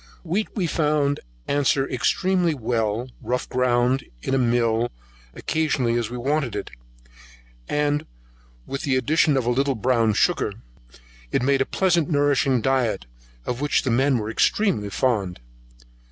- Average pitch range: Yes, average, 3.5 semitones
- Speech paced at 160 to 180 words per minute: No, average, 140 wpm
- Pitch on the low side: Yes, low, 130 Hz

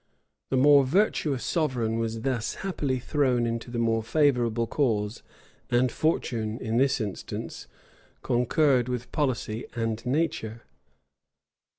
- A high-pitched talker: No, low, 125 Hz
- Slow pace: Yes, slow, 115 wpm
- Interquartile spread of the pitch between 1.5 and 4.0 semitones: Yes, average, 3.4 semitones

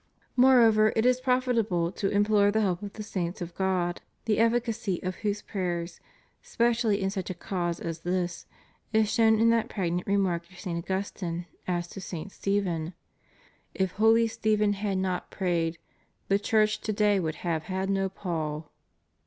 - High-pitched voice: Yes, high, 195 Hz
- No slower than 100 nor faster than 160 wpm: No, average, 170 wpm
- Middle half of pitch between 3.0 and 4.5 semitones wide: Yes, average, 3.6 semitones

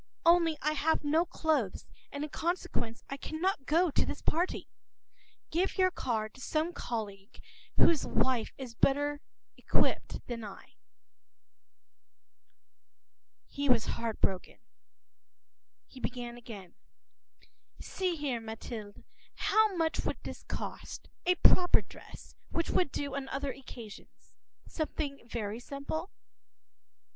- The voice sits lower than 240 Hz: No, very high, 280 Hz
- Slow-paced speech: Yes, slow, 120 wpm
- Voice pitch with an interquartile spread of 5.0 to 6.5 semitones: Yes, wide, 5.6 semitones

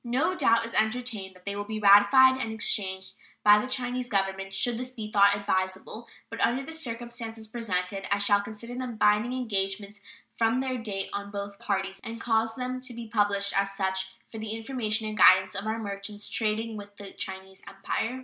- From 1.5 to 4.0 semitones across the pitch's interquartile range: Yes, average, 2.9 semitones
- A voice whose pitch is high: Yes, high, 215 Hz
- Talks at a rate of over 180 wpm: Yes, average, 190 wpm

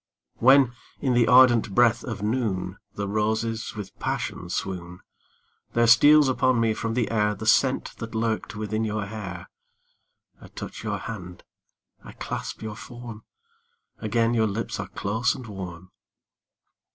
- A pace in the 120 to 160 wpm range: Yes, average, 145 wpm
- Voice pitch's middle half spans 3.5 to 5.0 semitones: No, narrow, 2.6 semitones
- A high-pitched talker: No, low, 110 Hz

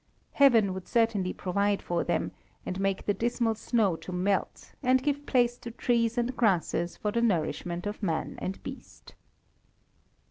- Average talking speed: Yes, average, 155 wpm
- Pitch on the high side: Yes, high, 210 Hz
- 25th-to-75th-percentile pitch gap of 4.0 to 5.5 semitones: Yes, average, 4.3 semitones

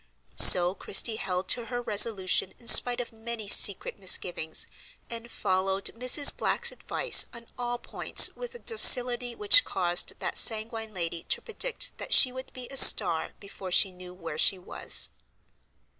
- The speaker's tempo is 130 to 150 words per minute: No, average, 160 wpm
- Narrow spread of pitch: No, average, 4.8 semitones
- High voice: Yes, high, 220 Hz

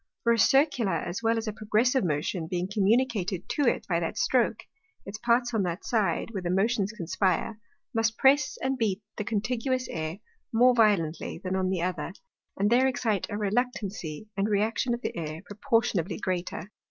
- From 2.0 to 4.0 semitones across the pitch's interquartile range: No, average, 4.4 semitones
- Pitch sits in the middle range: No, high, 210 Hz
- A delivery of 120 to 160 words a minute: No, average, 175 wpm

